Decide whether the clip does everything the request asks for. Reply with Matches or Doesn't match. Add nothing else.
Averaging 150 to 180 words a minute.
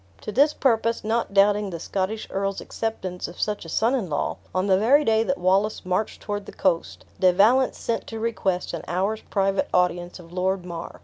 Doesn't match